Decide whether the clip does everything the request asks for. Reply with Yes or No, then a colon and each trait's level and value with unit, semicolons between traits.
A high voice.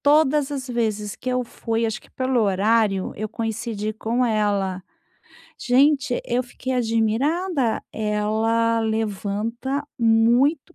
Yes: high, 230 Hz